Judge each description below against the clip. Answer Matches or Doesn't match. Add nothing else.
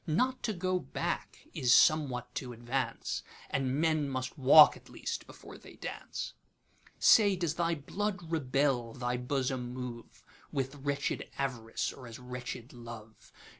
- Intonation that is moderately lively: Matches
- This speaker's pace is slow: Matches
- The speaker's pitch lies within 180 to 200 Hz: Doesn't match